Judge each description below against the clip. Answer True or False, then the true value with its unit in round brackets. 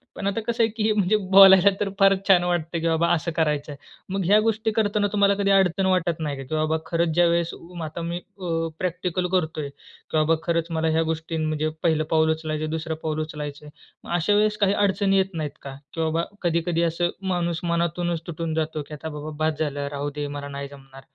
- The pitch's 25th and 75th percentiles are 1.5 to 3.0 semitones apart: False (3.4 semitones)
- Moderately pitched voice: True (165 Hz)